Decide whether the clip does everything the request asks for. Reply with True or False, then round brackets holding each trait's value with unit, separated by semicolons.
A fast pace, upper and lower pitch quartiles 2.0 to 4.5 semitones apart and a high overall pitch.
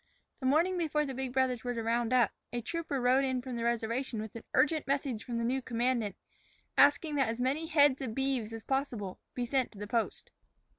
True (215 wpm; 2.9 semitones; 255 Hz)